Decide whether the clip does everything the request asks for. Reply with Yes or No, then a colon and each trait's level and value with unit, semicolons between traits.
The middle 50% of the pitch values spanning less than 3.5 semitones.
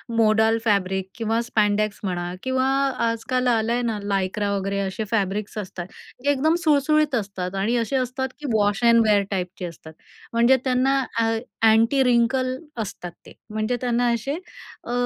No: average, 4.0 semitones